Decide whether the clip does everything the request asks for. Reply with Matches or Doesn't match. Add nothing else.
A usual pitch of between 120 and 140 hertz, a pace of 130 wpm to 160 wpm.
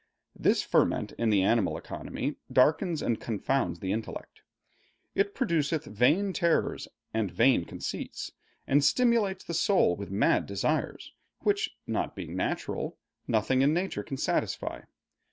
Matches